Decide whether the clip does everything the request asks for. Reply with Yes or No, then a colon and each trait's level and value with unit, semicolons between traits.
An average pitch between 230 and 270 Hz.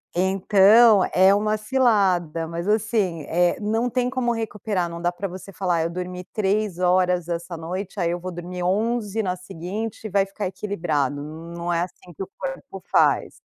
No: medium, 185 Hz